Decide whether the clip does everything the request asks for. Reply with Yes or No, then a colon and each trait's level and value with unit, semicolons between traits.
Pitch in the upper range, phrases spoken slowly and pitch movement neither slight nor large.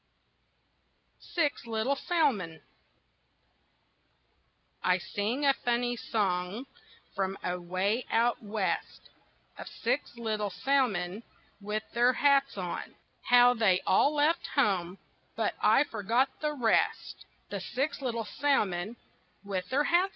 No: high, 230 Hz; slow, 115 wpm; wide, 5.9 semitones